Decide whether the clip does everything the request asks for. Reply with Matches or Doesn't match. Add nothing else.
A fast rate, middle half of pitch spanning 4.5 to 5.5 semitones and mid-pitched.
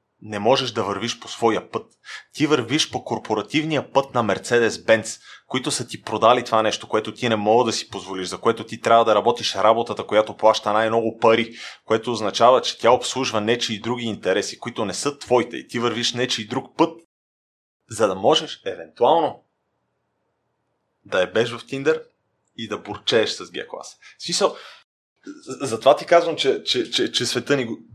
Doesn't match